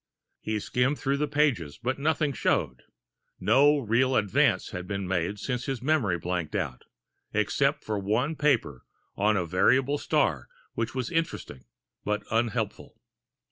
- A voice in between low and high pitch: No, low, 115 Hz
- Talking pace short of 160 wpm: Yes, average, 140 wpm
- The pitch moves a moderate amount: No, wide, 6.0 semitones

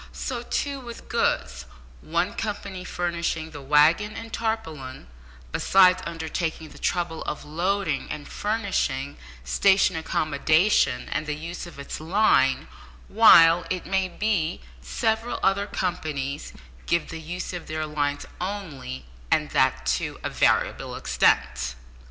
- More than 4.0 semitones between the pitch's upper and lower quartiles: Yes, average, 4.8 semitones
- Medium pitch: Yes, medium, 165 Hz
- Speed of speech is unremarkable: No, slow, 130 wpm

